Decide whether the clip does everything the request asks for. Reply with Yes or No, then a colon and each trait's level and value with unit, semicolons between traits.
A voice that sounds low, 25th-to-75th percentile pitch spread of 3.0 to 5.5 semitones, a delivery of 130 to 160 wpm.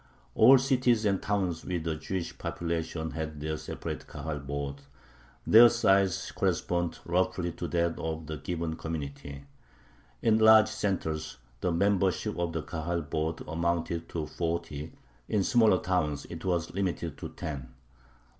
Yes: very low, 85 Hz; average, 3.3 semitones; average, 140 wpm